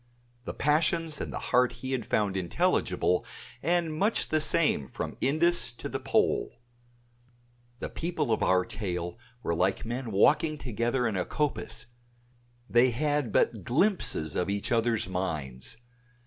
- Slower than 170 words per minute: Yes, average, 145 wpm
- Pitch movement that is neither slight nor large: No, wide, 7.8 semitones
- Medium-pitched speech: No, low, 120 Hz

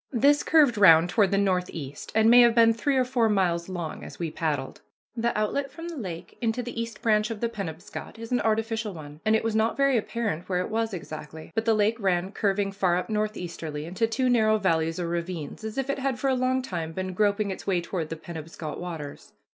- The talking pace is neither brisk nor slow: No, fast, 225 wpm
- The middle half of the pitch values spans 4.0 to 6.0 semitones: Yes, average, 5.0 semitones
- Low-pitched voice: No, high, 210 Hz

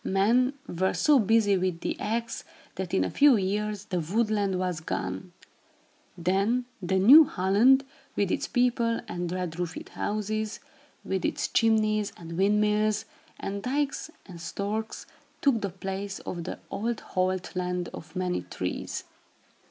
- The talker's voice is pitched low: No, high, 200 Hz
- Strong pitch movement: No, average, 3.4 semitones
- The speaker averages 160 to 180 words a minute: No, average, 145 wpm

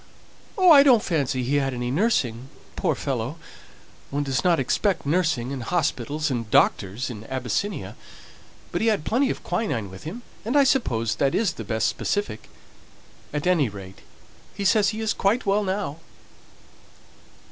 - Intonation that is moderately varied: No, wide, 8.9 semitones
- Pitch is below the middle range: No, medium, 145 Hz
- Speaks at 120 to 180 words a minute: Yes, average, 160 wpm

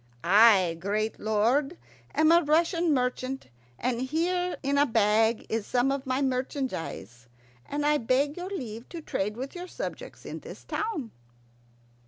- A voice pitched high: Yes, very high, 260 Hz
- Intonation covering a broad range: Yes, wide, 5.7 semitones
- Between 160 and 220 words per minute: No, average, 150 wpm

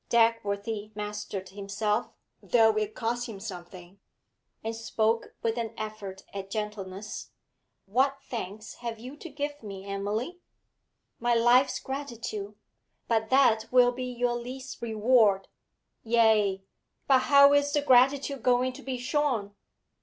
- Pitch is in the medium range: No, high, 225 Hz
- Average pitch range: Yes, average, 3.3 semitones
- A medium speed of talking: No, slow, 130 wpm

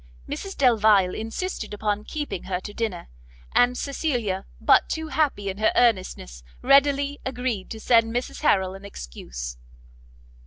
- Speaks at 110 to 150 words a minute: Yes, average, 140 wpm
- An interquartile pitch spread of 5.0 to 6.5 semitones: Yes, wide, 5.6 semitones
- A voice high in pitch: Yes, high, 220 Hz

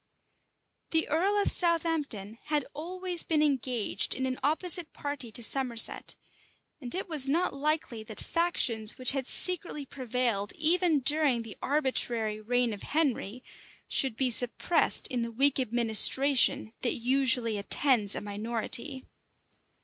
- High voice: Yes, very high, 260 Hz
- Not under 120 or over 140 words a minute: Yes, slow, 135 wpm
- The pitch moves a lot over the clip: No, average, 4.8 semitones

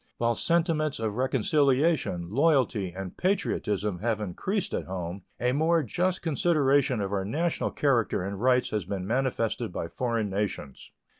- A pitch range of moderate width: No, wide, 6.8 semitones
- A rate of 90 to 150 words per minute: Yes, average, 145 wpm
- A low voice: Yes, low, 120 Hz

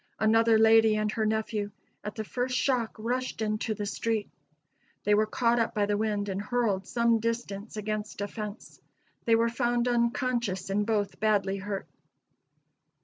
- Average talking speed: Yes, average, 160 wpm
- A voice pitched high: Yes, high, 220 Hz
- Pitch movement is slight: Yes, narrow, 2.1 semitones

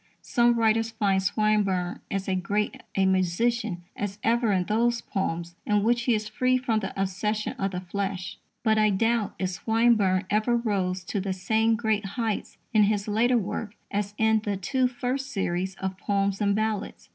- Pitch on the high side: Yes, high, 210 Hz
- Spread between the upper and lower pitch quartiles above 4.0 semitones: No, average, 2.9 semitones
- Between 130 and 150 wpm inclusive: No, average, 175 wpm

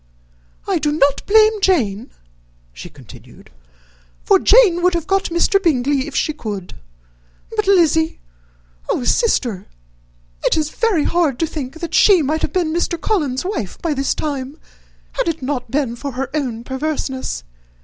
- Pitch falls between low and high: No, very high, 305 Hz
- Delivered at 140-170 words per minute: Yes, average, 155 wpm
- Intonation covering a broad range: No, average, 5.0 semitones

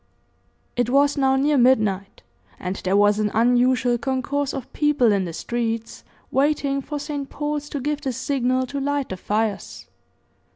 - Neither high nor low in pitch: No, very high, 260 Hz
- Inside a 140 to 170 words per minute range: Yes, average, 160 wpm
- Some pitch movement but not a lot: Yes, average, 4.0 semitones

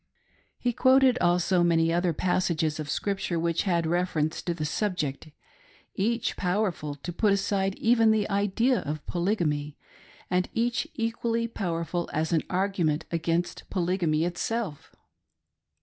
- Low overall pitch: No, medium, 180 Hz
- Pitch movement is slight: No, average, 4.2 semitones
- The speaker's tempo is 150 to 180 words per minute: No, slow, 135 wpm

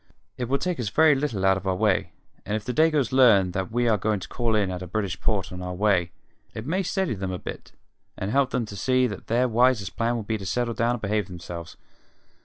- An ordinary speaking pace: No, fast, 250 wpm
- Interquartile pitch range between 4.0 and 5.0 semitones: Yes, average, 4.6 semitones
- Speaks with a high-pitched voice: No, low, 110 Hz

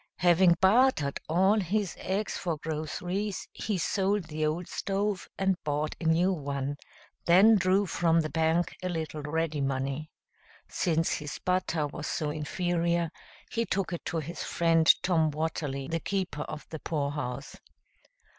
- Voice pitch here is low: No, medium, 165 Hz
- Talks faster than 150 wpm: No, average, 145 wpm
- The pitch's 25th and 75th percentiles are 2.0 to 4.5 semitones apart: Yes, average, 3.4 semitones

